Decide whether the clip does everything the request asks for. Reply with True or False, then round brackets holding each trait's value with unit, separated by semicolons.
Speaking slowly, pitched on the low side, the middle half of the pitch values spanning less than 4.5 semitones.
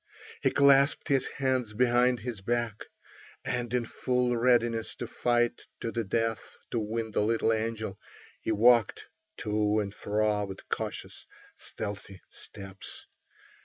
True (130 wpm; 115 Hz; 2.4 semitones)